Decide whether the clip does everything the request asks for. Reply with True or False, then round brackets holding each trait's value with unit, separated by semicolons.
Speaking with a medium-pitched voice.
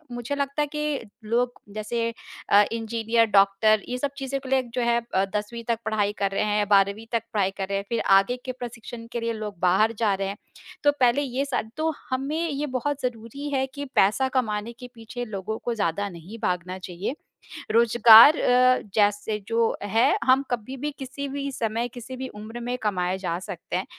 False (230 Hz)